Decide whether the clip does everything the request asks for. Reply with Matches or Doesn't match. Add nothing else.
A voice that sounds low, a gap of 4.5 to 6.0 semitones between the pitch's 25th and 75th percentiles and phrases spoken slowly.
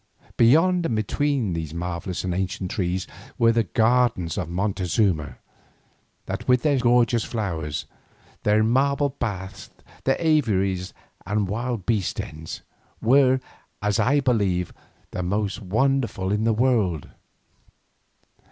Matches